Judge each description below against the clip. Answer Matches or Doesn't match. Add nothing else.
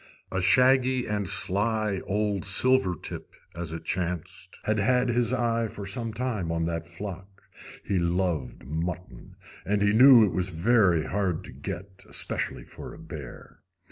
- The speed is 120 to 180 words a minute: Matches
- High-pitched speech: Doesn't match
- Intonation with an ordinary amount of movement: Matches